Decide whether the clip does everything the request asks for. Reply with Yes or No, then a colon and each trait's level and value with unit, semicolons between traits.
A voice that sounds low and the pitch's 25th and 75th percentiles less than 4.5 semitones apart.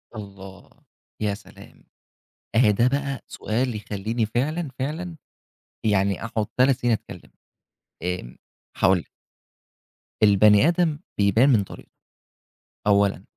No: low, 110 Hz; average, 4.8 semitones